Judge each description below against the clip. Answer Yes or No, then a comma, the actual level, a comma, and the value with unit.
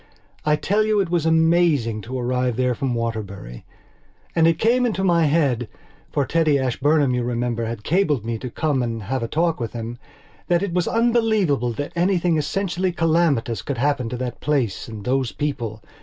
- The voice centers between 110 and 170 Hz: Yes, medium, 140 Hz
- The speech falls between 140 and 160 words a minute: No, average, 180 wpm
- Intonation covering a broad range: Yes, wide, 6.1 semitones